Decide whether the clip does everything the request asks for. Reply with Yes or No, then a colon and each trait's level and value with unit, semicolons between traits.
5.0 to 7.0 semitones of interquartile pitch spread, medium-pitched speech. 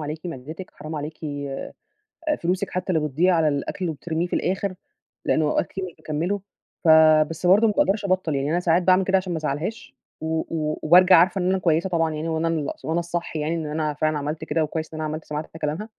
No: average, 2.8 semitones; medium, 160 Hz